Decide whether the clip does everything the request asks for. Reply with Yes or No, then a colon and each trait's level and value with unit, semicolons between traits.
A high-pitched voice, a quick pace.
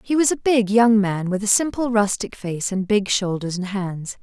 Yes: high, 210 Hz; fast, 225 wpm